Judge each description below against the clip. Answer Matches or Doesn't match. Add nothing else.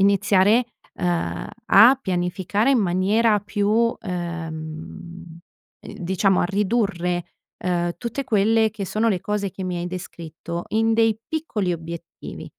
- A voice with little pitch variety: Doesn't match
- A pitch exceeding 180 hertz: Matches